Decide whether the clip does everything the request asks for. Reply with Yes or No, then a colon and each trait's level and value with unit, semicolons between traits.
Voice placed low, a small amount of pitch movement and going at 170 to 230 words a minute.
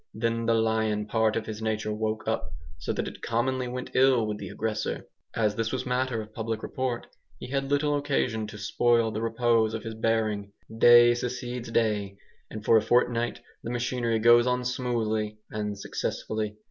Yes: low, 115 Hz; narrow, 2.0 semitones; average, 180 wpm